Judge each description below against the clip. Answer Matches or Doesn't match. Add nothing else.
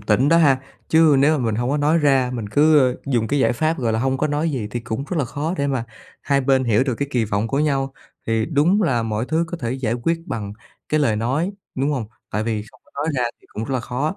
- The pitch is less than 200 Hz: Matches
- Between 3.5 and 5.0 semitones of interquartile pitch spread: Matches